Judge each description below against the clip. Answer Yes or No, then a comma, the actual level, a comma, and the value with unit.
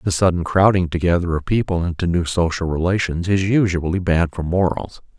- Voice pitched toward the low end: Yes, very low, 90 Hz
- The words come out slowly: No, average, 175 wpm